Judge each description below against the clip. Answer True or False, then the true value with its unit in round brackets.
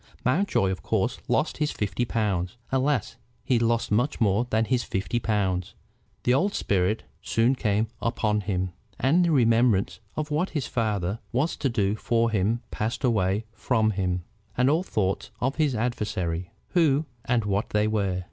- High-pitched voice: False (115 Hz)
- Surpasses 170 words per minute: False (165 wpm)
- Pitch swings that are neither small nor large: True (4.1 semitones)